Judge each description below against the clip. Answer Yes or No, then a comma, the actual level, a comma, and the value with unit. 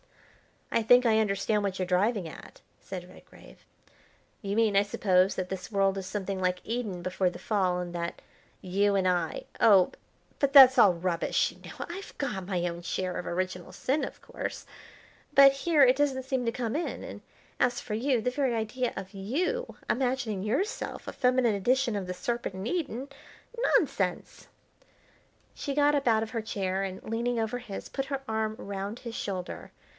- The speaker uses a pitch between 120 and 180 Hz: No, high, 220 Hz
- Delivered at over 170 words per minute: Yes, average, 180 wpm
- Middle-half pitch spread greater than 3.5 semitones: Yes, average, 5.1 semitones